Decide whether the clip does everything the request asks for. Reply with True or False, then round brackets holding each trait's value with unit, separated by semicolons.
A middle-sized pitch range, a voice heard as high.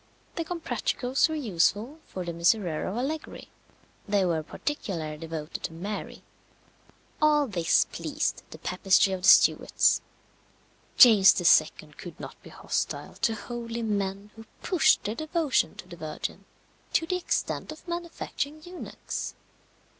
False (8.9 semitones; 220 Hz)